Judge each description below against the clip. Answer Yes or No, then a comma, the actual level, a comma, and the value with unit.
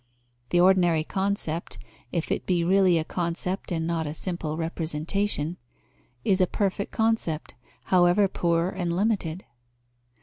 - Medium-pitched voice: Yes, medium, 175 Hz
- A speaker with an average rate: No, slow, 130 wpm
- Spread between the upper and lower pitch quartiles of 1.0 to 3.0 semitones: Yes, narrow, 2.6 semitones